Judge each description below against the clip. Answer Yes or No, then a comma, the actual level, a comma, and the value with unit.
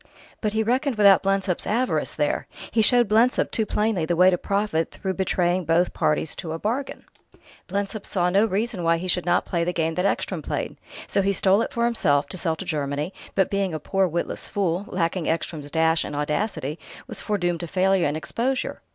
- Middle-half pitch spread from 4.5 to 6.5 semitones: No, average, 3.9 semitones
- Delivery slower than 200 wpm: No, fast, 205 wpm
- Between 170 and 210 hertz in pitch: Yes, medium, 185 Hz